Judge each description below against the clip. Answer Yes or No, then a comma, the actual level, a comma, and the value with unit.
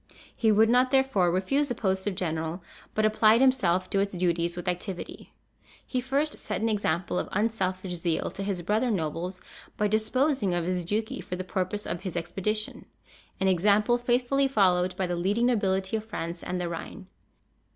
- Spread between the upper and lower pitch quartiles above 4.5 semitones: No, average, 3.8 semitones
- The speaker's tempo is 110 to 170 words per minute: No, average, 180 wpm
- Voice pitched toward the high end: Yes, high, 195 Hz